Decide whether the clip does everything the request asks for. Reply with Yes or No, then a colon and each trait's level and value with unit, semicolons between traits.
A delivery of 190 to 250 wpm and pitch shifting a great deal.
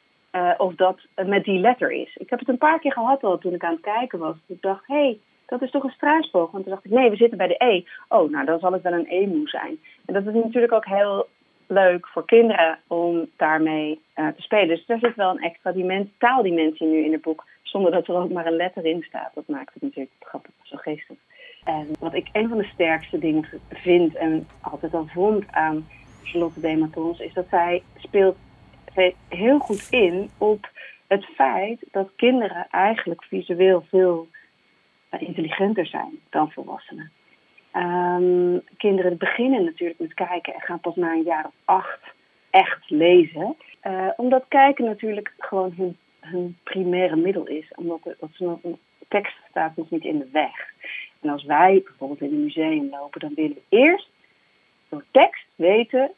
Yes: average, 195 wpm; wide, 5.7 semitones